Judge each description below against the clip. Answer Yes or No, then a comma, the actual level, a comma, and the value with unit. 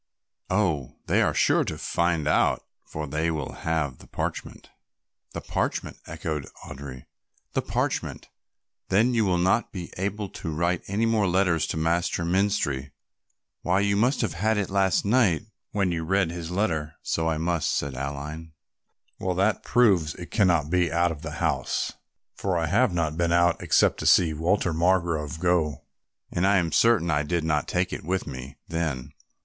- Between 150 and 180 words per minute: Yes, average, 175 wpm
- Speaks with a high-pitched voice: No, very low, 85 Hz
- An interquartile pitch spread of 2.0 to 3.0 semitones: No, average, 3.6 semitones